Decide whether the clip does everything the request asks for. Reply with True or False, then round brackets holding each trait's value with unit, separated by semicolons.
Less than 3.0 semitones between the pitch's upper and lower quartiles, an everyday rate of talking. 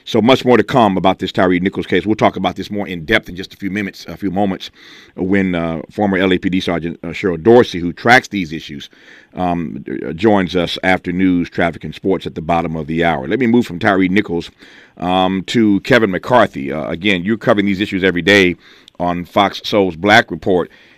False (2.6 semitones; 210 wpm)